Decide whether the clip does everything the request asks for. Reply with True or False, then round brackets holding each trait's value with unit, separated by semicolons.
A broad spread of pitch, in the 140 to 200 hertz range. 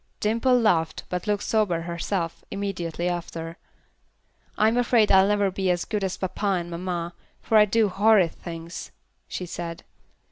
False (3.6 semitones; 190 Hz)